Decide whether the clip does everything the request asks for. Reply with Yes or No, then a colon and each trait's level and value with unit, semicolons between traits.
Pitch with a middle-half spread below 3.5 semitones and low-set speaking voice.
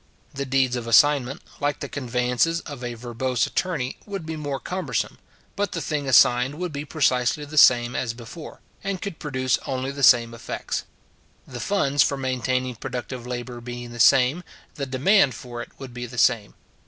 Yes: average, 3.1 semitones; low, 130 Hz